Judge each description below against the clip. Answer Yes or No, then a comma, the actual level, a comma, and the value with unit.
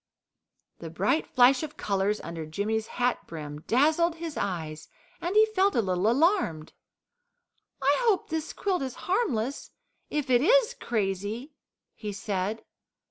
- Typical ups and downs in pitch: No, wide, 8.7 semitones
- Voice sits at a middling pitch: No, high, 245 Hz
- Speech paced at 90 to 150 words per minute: Yes, slow, 135 wpm